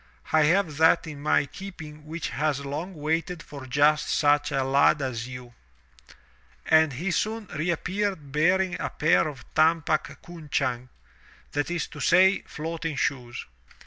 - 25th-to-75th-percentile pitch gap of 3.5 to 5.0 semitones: No, average, 3.1 semitones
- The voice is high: No, medium, 155 Hz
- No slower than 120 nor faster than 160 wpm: Yes, average, 145 wpm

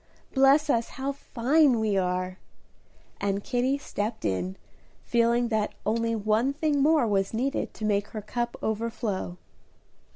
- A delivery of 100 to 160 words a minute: Yes, slow, 135 wpm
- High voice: Yes, high, 230 Hz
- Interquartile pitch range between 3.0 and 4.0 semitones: No, average, 4.5 semitones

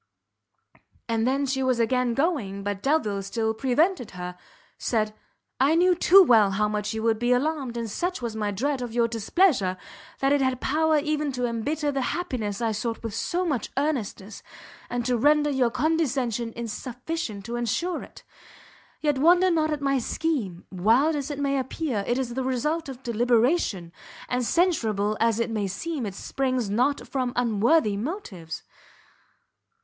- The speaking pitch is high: Yes, very high, 250 Hz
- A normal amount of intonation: Yes, average, 5.0 semitones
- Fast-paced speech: No, average, 165 wpm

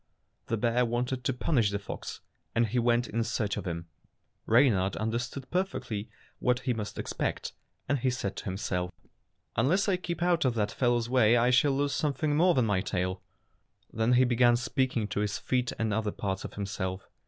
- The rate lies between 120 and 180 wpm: No, average, 190 wpm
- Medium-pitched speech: No, low, 120 Hz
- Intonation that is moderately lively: Yes, average, 3.7 semitones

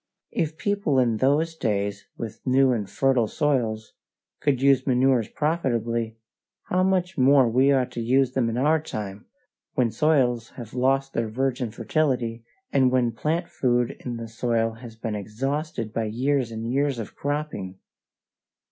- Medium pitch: No, low, 125 Hz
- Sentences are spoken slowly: No, average, 155 wpm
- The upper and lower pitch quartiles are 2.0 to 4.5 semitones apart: Yes, average, 3.5 semitones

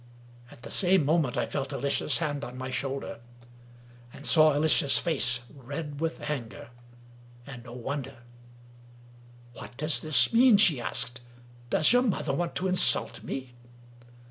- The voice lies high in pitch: No, medium, 140 Hz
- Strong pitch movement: No, average, 3.8 semitones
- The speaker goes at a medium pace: Yes, average, 145 wpm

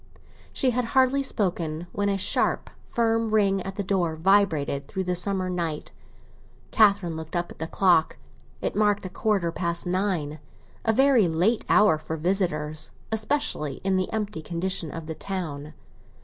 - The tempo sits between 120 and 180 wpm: Yes, average, 155 wpm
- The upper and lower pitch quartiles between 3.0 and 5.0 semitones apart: Yes, average, 4.2 semitones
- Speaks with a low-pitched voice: No, medium, 185 Hz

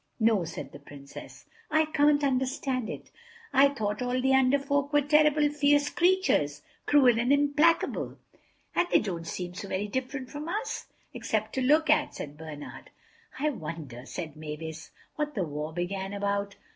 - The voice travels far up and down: Yes, wide, 8.6 semitones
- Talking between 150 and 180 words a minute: Yes, average, 160 wpm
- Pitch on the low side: No, very high, 255 Hz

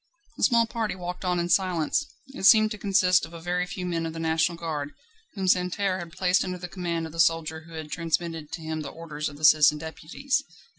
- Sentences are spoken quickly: Yes, fast, 230 wpm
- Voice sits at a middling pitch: Yes, medium, 170 Hz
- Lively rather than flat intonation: No, narrow, 2.4 semitones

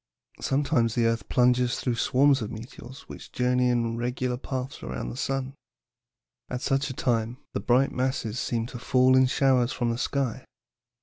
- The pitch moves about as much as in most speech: No, narrow, 1.9 semitones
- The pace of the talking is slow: No, average, 170 wpm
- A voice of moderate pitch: No, low, 125 Hz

